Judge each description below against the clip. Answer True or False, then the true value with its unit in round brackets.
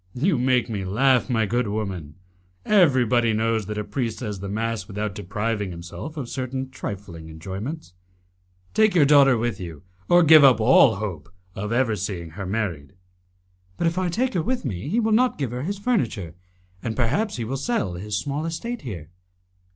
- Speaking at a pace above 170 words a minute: True (180 wpm)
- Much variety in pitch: True (6.3 semitones)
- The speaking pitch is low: True (115 Hz)